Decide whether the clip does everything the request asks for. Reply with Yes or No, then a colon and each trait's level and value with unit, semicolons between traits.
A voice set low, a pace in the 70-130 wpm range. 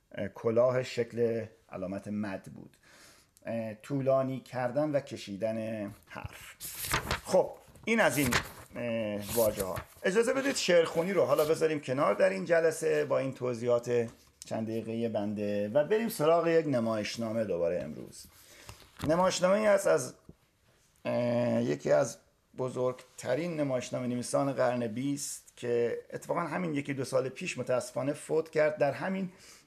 Yes: low, 130 Hz; average, 125 wpm